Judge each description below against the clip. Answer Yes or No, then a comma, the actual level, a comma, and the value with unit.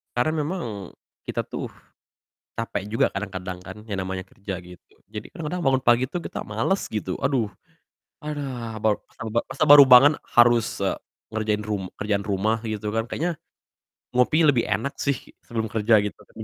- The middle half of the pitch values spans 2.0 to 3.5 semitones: No, average, 4.5 semitones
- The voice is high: No, low, 115 Hz